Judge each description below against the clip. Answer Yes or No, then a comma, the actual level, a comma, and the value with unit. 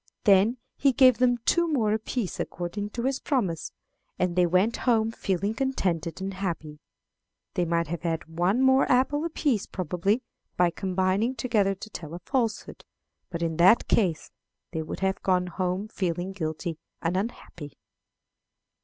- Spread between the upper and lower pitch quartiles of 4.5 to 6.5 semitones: Yes, average, 5.1 semitones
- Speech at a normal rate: Yes, average, 155 wpm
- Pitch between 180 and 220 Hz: Yes, high, 190 Hz